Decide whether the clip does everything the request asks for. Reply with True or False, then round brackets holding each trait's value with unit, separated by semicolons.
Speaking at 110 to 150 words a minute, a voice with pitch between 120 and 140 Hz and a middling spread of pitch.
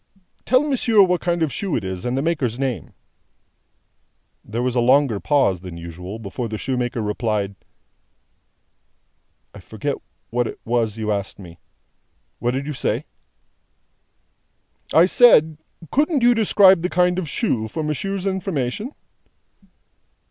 False (140 wpm; 135 Hz; 8.5 semitones)